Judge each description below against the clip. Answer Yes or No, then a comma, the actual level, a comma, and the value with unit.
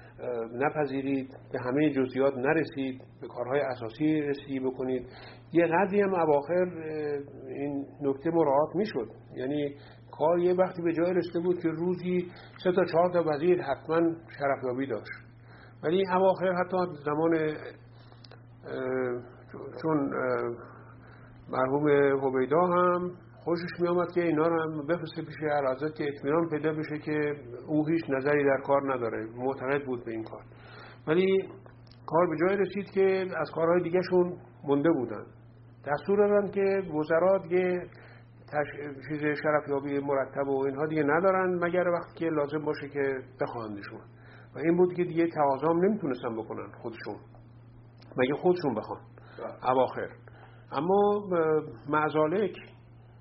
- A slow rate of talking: Yes, slow, 130 wpm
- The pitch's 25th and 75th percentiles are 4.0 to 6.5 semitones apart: Yes, average, 5.1 semitones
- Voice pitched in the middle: Yes, medium, 145 Hz